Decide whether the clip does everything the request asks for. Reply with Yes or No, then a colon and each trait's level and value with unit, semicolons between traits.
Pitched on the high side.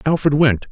No: low, 135 Hz